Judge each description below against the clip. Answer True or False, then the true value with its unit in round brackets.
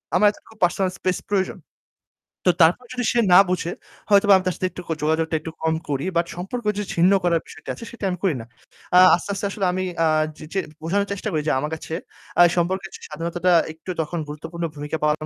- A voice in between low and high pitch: True (175 Hz)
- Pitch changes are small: False (3.2 semitones)